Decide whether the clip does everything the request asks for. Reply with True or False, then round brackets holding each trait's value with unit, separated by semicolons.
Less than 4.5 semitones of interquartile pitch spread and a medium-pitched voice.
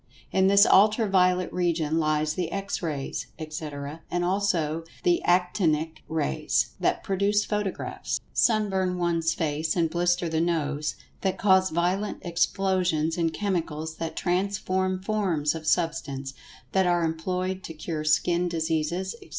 True (2.9 semitones; 175 Hz)